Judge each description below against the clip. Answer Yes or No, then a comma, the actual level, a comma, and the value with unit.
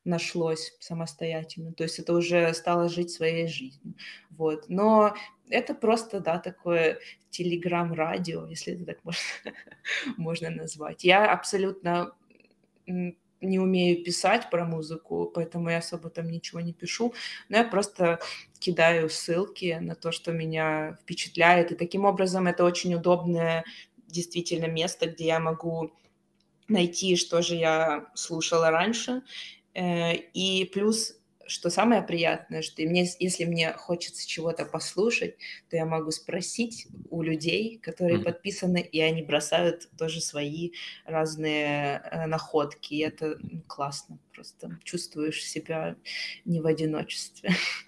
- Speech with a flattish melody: Yes, narrow, 1.9 semitones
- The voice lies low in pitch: No, medium, 170 Hz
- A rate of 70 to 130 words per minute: Yes, average, 125 wpm